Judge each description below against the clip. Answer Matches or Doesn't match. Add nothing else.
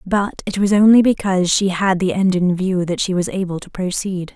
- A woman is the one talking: Matches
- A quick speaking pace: Matches